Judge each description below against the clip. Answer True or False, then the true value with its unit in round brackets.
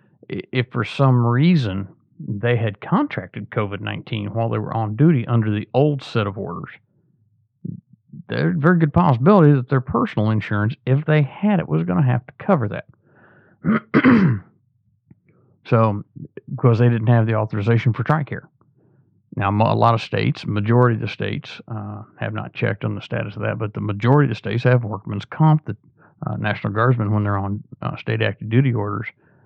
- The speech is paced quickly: False (180 wpm)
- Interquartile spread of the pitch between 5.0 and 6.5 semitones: True (5.3 semitones)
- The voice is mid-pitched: False (120 Hz)